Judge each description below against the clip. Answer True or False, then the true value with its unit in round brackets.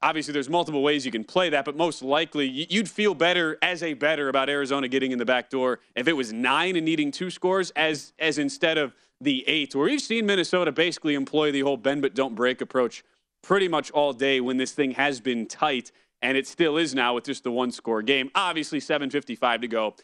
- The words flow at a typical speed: False (230 wpm)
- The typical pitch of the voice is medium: True (145 Hz)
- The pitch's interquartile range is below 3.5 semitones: False (3.9 semitones)